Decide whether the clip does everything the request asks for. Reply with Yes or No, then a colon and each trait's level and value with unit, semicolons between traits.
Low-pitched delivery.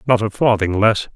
Yes: low, 110 Hz